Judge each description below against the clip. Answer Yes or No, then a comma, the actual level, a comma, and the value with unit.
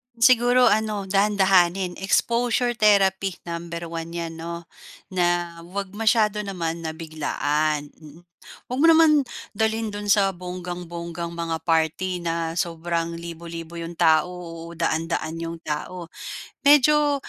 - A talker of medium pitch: Yes, medium, 175 Hz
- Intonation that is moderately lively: Yes, average, 3.7 semitones